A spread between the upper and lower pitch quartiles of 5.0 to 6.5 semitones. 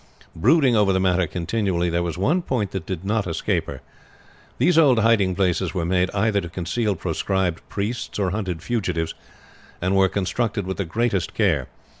No: average, 3.8 semitones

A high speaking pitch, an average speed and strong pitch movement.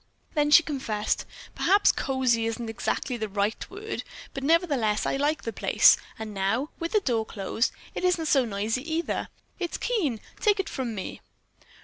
Yes: very high, 260 Hz; average, 165 wpm; wide, 6.7 semitones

